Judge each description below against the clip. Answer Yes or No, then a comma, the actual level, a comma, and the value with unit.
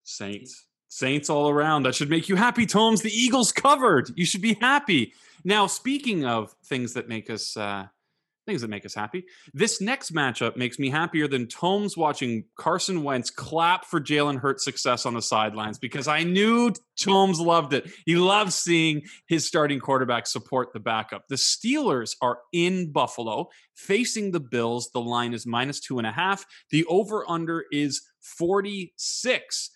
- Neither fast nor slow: Yes, average, 170 wpm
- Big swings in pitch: Yes, wide, 7.6 semitones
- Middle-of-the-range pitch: Yes, medium, 150 Hz